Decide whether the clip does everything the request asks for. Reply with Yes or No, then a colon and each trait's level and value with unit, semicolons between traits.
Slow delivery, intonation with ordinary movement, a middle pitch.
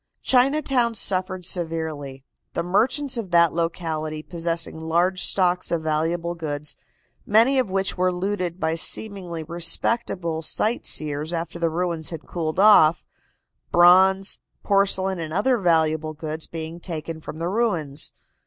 Yes: slow, 130 wpm; average, 3.1 semitones; medium, 170 Hz